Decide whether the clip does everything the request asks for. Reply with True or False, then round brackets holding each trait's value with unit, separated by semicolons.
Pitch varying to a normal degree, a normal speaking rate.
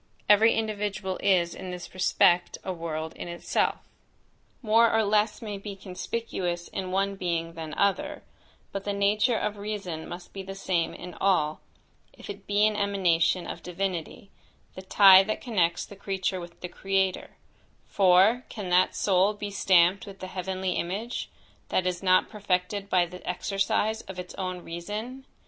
False (2.3 semitones; 165 wpm)